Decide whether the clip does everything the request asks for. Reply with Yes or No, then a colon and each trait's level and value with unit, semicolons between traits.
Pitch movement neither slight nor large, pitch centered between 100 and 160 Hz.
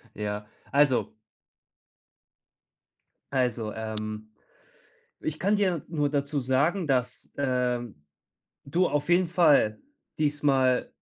Yes: average, 4.0 semitones; medium, 140 Hz